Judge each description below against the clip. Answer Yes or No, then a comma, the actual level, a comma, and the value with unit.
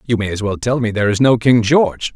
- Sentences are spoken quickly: Yes, fast, 305 wpm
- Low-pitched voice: Yes, low, 115 Hz